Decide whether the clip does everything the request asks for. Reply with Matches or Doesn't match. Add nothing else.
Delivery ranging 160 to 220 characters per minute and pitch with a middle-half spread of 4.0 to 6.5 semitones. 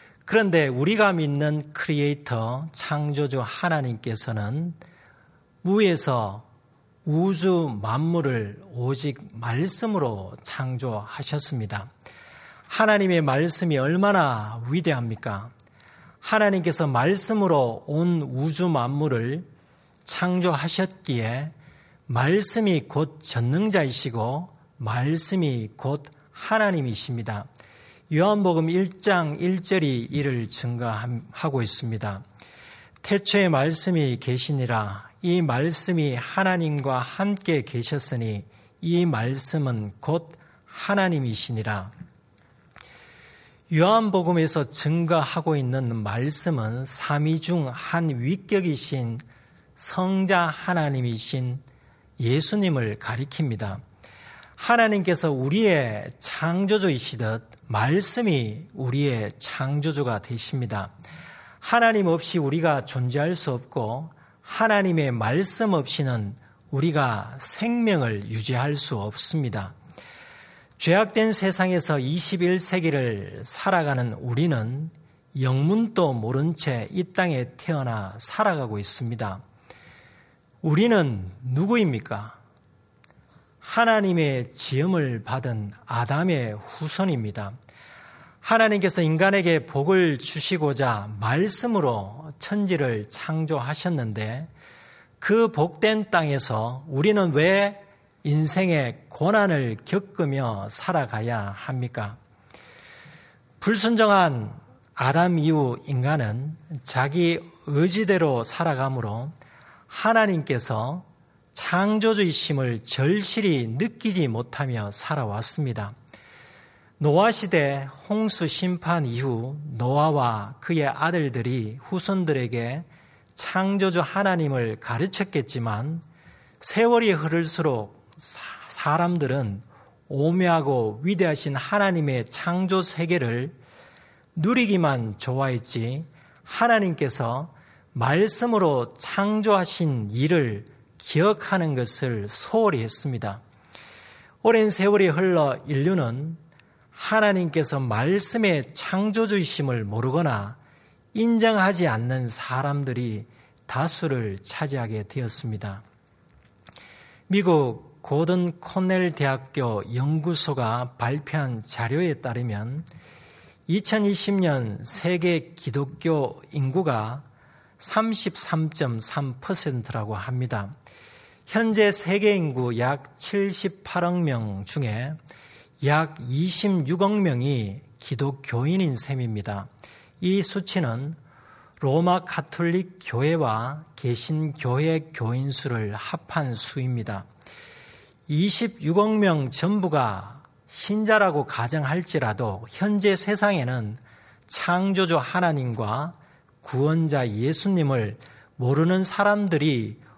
Matches